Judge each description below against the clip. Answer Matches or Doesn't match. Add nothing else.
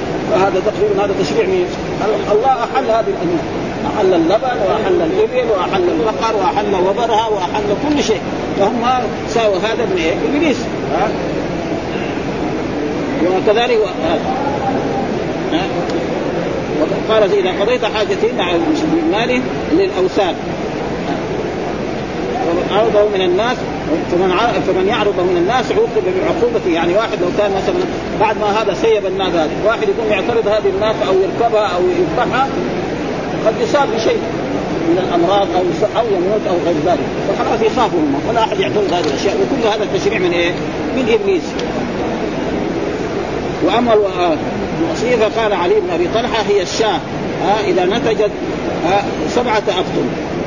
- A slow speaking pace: Doesn't match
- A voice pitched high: Matches